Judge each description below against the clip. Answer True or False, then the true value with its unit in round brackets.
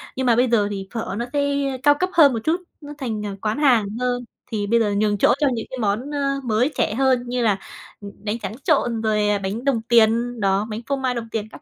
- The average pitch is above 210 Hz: True (235 Hz)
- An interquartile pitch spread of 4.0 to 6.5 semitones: False (3.6 semitones)